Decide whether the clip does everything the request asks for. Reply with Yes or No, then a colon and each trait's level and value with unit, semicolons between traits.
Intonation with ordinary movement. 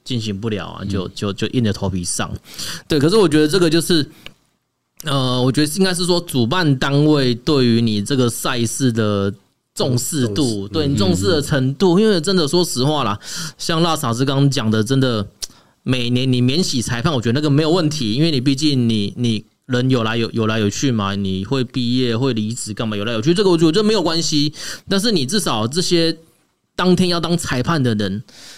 No: wide, 6.2 semitones